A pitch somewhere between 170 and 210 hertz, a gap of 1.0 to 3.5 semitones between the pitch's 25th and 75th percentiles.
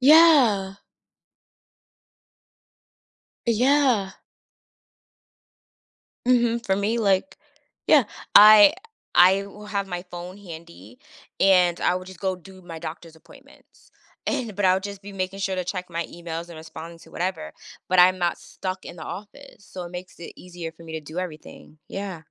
Yes: medium, 185 Hz; average, 2.9 semitones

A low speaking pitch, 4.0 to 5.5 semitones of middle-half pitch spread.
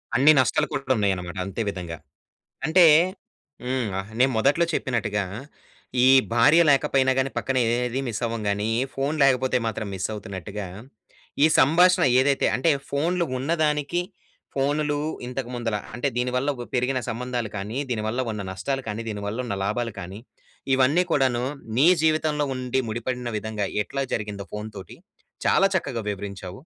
Yes: low, 125 Hz; average, 4.6 semitones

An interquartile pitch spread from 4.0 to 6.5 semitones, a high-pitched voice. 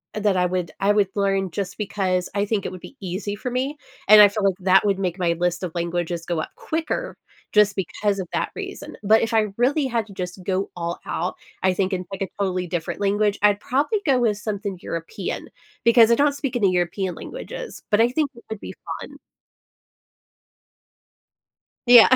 No: average, 3.5 semitones; high, 200 Hz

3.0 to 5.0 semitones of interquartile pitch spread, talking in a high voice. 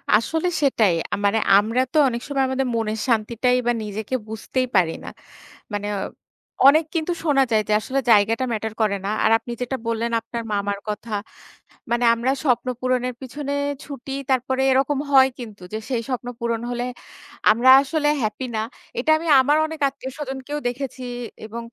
Yes: average, 3.3 semitones; high, 245 Hz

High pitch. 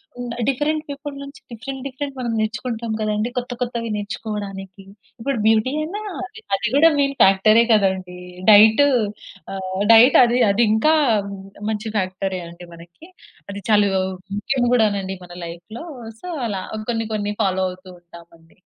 Yes: high, 215 Hz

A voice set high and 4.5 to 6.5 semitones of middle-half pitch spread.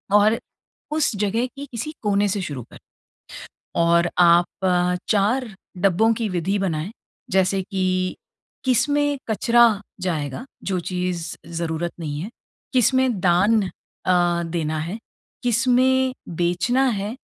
Yes: high, 195 Hz; average, 5.3 semitones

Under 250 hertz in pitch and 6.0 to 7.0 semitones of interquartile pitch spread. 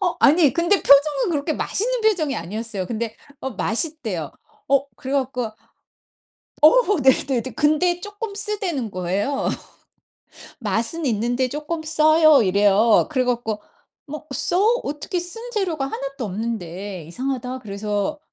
No: very high, 275 Hz; wide, 6.6 semitones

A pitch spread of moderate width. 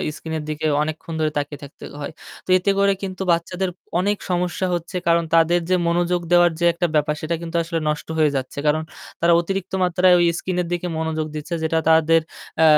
No: narrow, 2.2 semitones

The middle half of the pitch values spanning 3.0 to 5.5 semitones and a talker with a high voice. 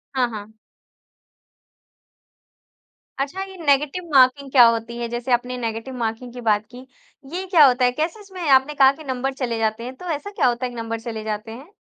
Yes: average, 3.3 semitones; very high, 250 Hz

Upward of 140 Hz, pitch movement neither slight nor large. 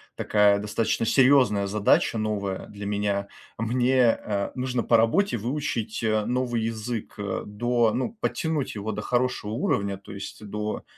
No: low, 110 Hz; average, 3.1 semitones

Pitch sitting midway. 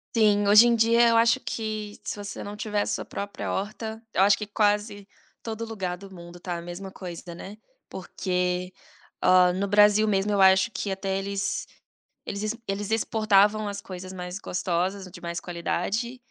No: high, 200 Hz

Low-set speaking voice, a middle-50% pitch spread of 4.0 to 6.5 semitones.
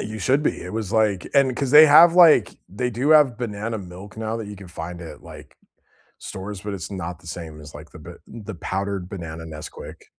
Yes: low, 100 Hz; average, 5.3 semitones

